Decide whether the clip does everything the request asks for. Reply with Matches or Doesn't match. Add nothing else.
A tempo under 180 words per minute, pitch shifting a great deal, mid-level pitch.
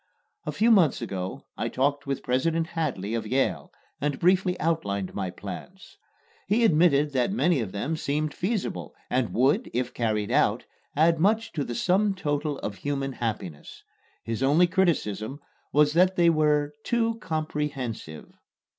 Matches